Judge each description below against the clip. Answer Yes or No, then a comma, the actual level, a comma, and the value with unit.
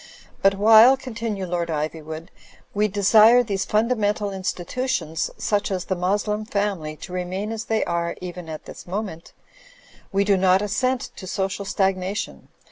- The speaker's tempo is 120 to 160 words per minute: Yes, average, 150 wpm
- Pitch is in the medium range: No, high, 195 Hz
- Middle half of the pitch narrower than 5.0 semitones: Yes, average, 2.9 semitones